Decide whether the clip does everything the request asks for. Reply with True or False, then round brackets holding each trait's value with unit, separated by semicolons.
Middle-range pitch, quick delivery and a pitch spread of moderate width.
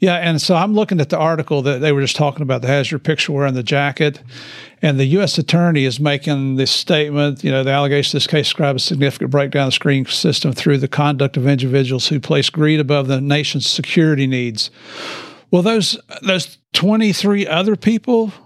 True (145 Hz; 210 wpm; 3.0 semitones)